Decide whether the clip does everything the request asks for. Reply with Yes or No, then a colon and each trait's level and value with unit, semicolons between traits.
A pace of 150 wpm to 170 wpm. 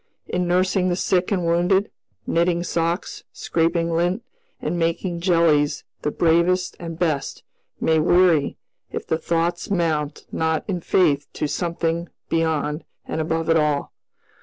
No: slow, 135 wpm